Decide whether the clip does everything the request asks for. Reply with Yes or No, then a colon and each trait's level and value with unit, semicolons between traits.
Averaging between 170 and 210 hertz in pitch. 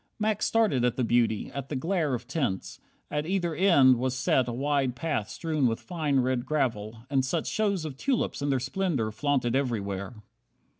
No: low, 135 Hz